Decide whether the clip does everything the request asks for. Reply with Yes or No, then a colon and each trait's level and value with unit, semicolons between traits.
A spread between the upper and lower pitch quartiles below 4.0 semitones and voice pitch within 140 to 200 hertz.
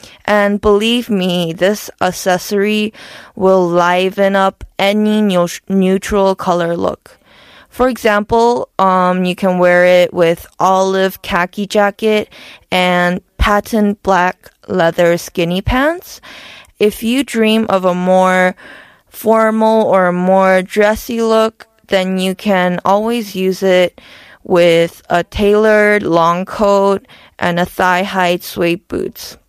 Yes: average, 2.7 semitones; high, 190 Hz